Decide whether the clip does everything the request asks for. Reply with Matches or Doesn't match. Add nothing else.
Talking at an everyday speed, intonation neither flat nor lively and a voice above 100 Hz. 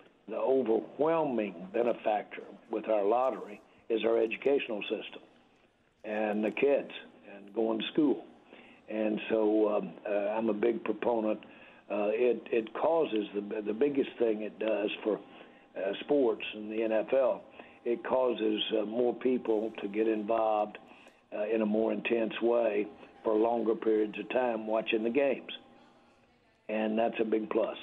Doesn't match